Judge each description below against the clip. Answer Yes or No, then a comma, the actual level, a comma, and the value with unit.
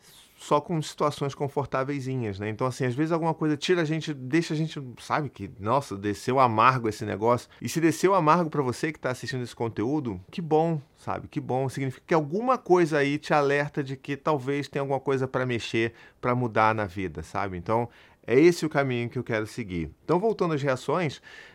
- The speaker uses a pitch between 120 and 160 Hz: Yes, low, 135 Hz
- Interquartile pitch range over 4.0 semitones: Yes, average, 4.5 semitones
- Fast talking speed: Yes, fast, 205 wpm